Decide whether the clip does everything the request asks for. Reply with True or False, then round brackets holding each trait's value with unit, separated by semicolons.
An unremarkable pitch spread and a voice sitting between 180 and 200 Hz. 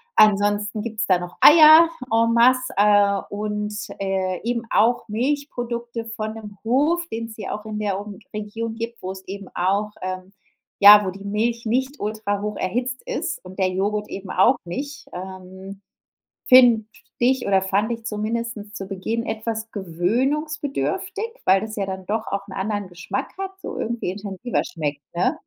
False (3.2 semitones; 210 Hz)